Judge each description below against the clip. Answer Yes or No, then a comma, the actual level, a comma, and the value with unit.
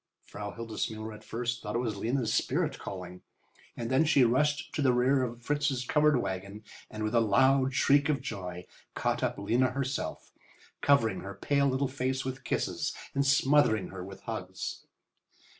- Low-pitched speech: Yes, low, 125 Hz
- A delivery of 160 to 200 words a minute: Yes, average, 170 wpm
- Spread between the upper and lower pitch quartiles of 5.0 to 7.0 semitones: No, average, 4.3 semitones